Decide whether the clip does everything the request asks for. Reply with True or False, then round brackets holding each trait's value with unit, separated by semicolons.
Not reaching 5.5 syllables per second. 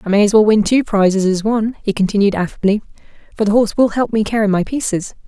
False (6.7 syllables/s)